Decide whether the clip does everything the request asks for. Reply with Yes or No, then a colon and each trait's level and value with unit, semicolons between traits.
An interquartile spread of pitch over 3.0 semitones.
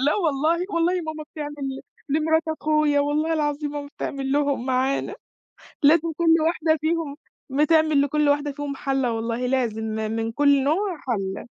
No: average, 2.7 semitones